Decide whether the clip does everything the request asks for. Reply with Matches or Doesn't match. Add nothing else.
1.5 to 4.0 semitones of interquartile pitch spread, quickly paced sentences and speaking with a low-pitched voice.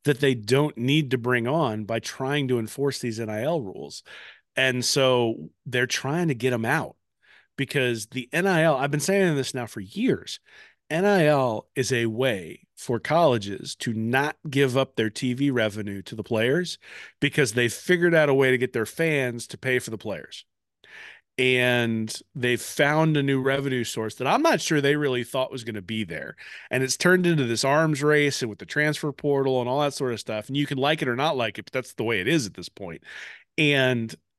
Matches